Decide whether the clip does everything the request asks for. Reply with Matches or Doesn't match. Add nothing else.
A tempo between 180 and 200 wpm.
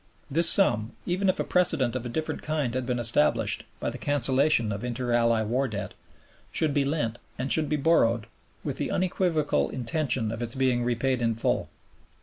Matches